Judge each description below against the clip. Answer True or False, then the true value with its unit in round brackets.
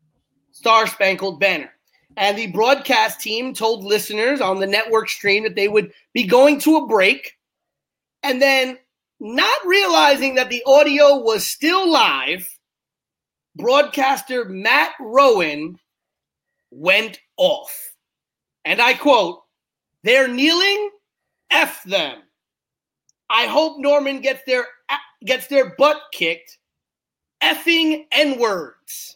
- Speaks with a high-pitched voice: True (255 Hz)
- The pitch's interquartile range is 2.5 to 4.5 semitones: False (5.3 semitones)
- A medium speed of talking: False (115 wpm)